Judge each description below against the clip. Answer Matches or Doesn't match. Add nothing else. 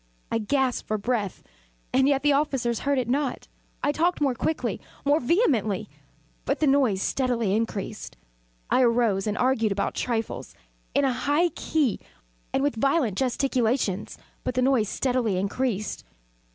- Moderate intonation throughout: Matches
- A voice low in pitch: Doesn't match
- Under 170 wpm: Matches